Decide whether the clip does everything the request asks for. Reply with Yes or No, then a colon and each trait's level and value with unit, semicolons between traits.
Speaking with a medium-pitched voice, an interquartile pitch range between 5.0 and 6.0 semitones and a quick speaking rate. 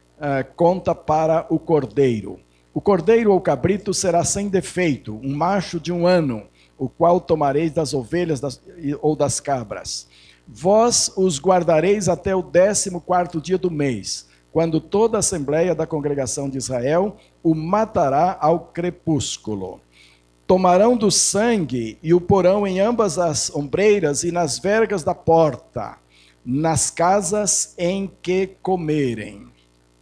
No: medium, 165 Hz; wide, 5.4 semitones; average, 135 wpm